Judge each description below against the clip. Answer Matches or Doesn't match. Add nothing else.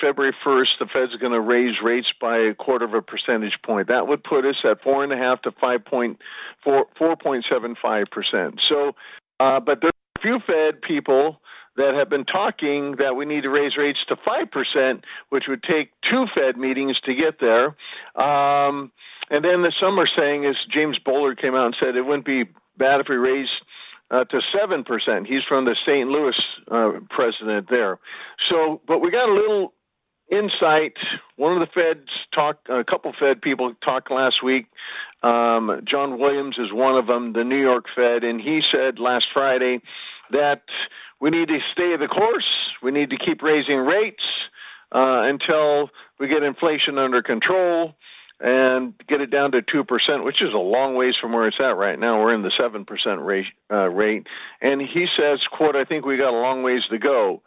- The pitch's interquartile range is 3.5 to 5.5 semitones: Doesn't match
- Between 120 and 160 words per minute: Doesn't match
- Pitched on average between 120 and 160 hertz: Matches